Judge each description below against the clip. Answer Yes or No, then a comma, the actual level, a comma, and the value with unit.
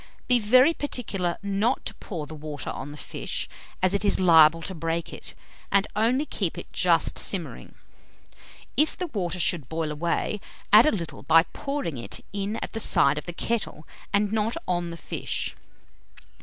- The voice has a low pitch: No, high, 190 Hz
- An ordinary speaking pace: Yes, average, 175 wpm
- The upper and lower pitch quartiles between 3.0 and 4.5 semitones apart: No, average, 5.2 semitones